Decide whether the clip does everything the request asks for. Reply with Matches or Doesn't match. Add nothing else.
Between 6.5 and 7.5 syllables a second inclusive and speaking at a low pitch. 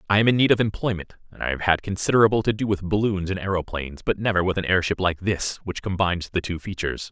Matches